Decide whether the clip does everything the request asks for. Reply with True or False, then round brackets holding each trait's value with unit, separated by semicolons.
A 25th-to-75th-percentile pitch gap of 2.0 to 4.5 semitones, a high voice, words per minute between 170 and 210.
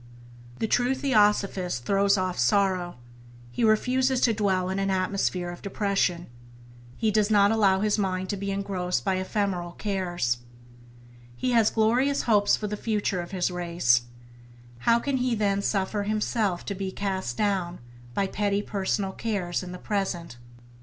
False (2.5 semitones; 200 Hz; 155 wpm)